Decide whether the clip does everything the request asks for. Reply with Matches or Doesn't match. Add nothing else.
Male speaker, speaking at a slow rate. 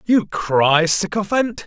Matches